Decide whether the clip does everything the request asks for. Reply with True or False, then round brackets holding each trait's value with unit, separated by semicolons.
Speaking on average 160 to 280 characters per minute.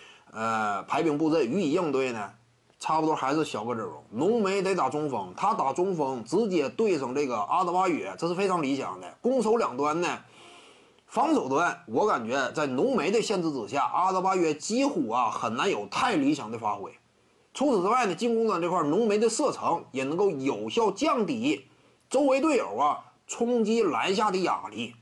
True (275 characters per minute)